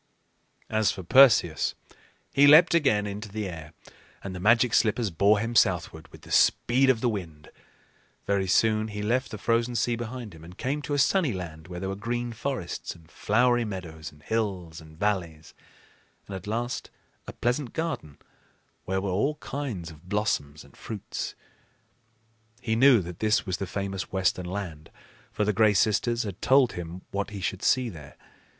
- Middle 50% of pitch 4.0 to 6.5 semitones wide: Yes, average, 5.0 semitones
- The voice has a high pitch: No, low, 105 Hz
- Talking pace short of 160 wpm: No, average, 175 wpm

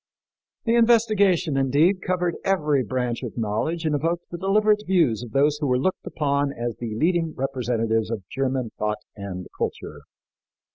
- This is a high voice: No, medium, 140 Hz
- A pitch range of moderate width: No, wide, 6.8 semitones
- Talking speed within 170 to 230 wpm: No, average, 155 wpm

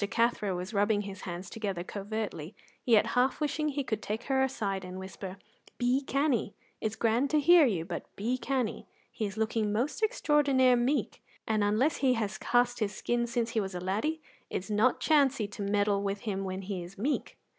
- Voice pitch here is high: Yes, high, 220 Hz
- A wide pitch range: No, average, 4.5 semitones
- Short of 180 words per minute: No, average, 190 wpm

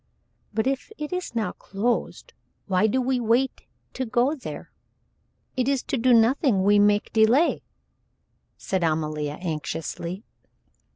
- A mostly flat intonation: No, average, 5.2 semitones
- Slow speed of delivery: Yes, slow, 130 wpm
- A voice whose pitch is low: No, high, 225 Hz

